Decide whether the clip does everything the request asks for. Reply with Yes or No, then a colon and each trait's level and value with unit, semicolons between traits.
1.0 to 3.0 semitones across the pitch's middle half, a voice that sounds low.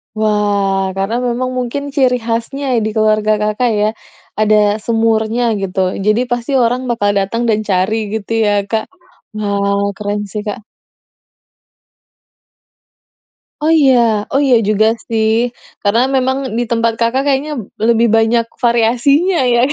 No: narrow, 2.5 semitones; high, 225 Hz